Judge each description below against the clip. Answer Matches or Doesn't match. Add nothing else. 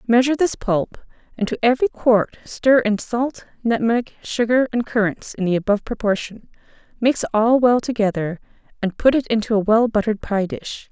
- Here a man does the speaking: Doesn't match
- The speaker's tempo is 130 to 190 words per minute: Matches